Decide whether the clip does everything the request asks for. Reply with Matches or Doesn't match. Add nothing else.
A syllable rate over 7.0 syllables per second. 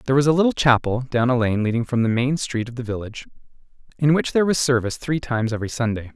Matches